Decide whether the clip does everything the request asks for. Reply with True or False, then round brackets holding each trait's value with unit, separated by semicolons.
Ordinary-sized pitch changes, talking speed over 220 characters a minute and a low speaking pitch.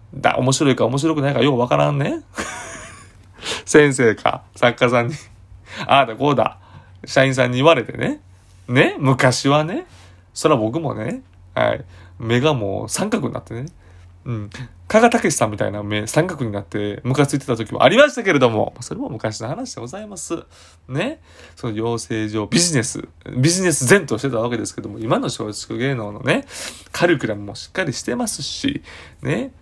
False (5.8 semitones; 330 characters per minute; 120 Hz)